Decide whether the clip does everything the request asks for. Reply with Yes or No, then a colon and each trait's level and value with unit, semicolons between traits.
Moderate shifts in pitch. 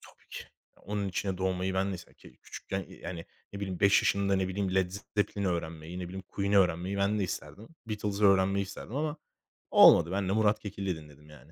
No: narrow, 1.8 semitones